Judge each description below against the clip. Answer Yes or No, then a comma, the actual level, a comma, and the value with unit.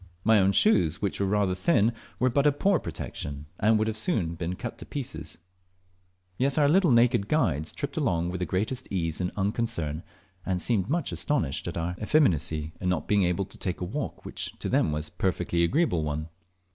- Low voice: Yes, very low, 95 Hz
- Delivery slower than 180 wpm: No, average, 200 wpm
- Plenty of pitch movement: Yes, wide, 6.3 semitones